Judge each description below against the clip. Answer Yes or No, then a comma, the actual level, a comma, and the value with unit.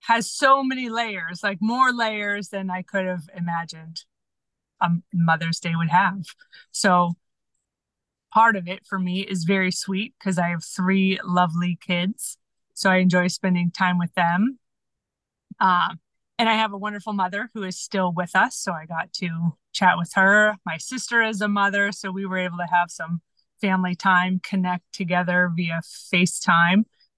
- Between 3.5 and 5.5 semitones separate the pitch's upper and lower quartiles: No, narrow, 2.5 semitones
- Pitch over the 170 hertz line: Yes, medium, 185 Hz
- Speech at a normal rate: Yes, average, 170 wpm